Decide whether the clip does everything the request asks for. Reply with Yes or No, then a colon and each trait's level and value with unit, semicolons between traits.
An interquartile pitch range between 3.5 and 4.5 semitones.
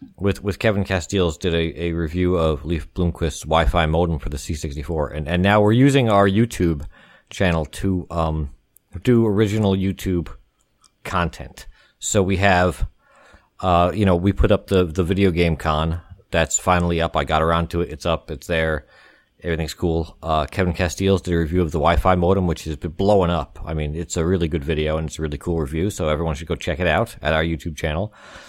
No: average, 3.0 semitones